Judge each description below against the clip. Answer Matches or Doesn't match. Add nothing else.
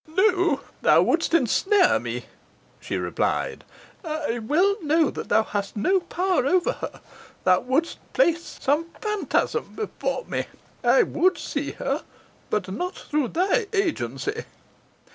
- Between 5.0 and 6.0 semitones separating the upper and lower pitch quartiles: Matches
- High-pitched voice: Matches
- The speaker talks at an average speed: Doesn't match